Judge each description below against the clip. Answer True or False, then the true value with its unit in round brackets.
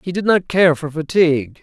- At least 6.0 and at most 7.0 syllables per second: False (5.2 syllables/s)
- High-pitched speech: False (160 Hz)